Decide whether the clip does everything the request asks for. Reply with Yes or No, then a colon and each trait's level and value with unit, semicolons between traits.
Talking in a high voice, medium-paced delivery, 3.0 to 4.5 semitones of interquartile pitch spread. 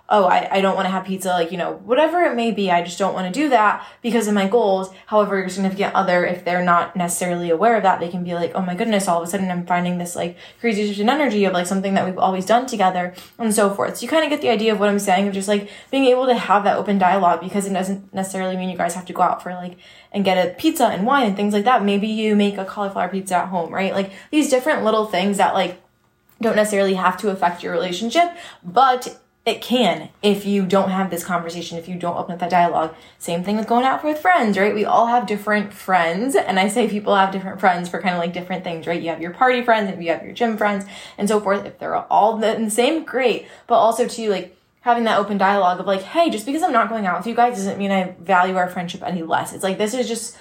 No: high, 195 Hz; fast, 270 wpm; average, 3.8 semitones